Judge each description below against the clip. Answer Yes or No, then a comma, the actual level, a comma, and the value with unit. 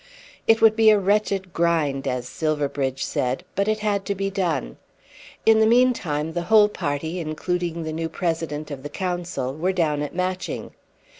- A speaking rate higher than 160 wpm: Yes, average, 170 wpm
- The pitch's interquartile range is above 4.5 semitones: Yes, average, 5.0 semitones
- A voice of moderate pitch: Yes, medium, 170 Hz